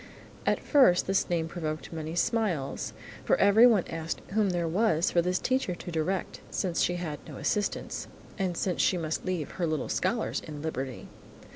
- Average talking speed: Yes, average, 170 wpm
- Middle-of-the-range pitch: Yes, medium, 175 Hz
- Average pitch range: Yes, average, 3.3 semitones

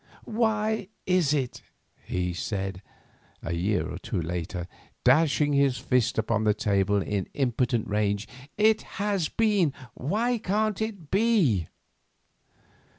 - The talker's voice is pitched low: Yes, low, 130 Hz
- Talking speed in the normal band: No, slow, 120 wpm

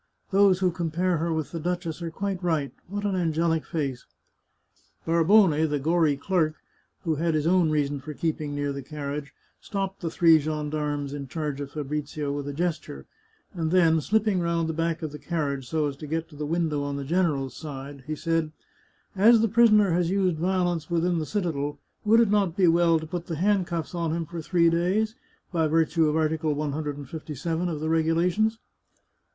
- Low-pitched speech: No, medium, 165 Hz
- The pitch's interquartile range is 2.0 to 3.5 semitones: Yes, average, 2.9 semitones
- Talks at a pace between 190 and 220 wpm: Yes, average, 195 wpm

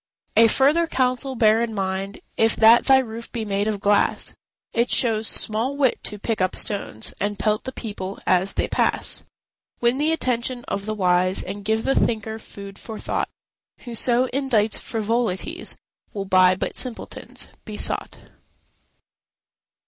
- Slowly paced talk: No, average, 155 wpm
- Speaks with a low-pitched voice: No, high, 220 Hz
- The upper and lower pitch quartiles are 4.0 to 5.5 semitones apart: No, average, 3.3 semitones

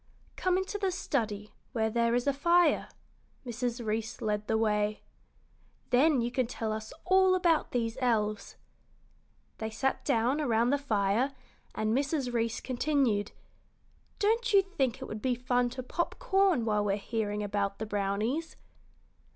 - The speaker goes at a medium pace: Yes, average, 150 wpm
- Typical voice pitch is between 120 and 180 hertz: No, high, 240 Hz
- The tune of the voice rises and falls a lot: No, average, 4.8 semitones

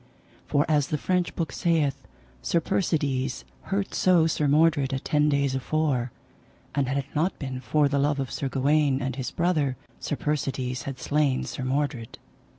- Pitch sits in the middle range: Yes, medium, 145 Hz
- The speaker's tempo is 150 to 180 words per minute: Yes, average, 170 wpm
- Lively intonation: No, narrow, 2.6 semitones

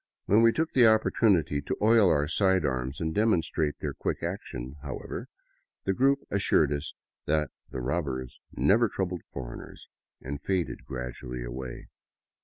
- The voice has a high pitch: No, very low, 80 Hz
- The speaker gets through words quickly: No, average, 145 wpm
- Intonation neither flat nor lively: No, wide, 7.2 semitones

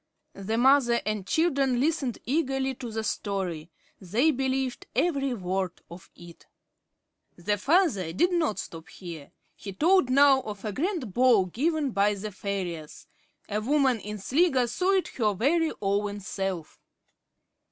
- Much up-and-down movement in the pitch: Yes, wide, 6.0 semitones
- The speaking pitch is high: Yes, high, 235 Hz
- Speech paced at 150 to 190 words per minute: No, average, 140 wpm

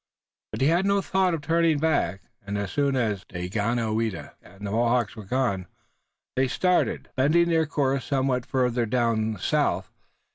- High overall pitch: No, low, 125 Hz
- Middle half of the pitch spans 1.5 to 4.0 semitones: No, wide, 5.5 semitones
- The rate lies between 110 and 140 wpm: No, average, 160 wpm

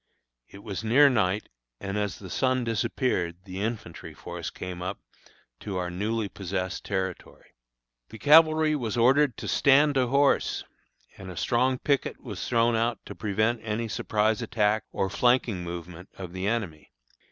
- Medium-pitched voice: No, low, 110 Hz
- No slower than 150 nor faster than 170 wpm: Yes, average, 155 wpm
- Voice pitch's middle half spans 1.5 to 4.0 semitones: No, average, 4.6 semitones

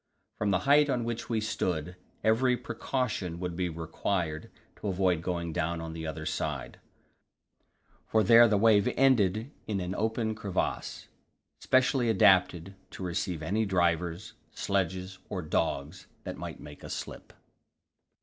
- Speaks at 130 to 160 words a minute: Yes, average, 140 wpm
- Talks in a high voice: No, very low, 95 Hz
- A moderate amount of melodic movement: Yes, average, 4.5 semitones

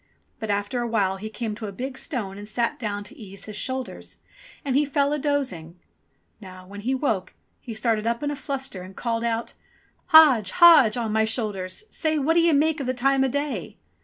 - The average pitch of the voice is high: Yes, high, 235 Hz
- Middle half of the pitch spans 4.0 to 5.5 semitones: Yes, average, 5.2 semitones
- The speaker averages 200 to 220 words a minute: Yes, fast, 205 wpm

